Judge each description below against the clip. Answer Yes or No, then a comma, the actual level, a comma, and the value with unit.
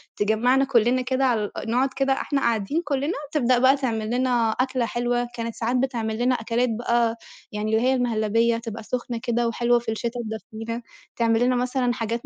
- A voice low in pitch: No, high, 240 Hz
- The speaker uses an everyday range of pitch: No, narrow, 2.0 semitones